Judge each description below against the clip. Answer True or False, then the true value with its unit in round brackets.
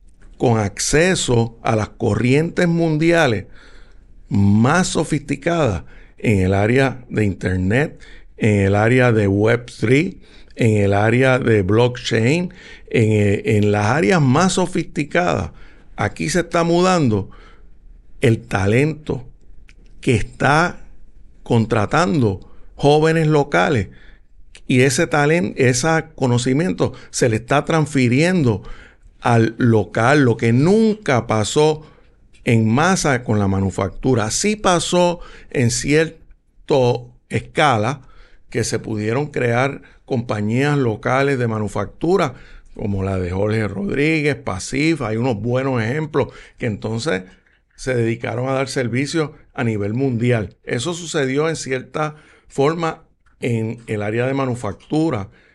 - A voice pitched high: False (125 Hz)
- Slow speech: True (110 wpm)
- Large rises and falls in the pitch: True (5.9 semitones)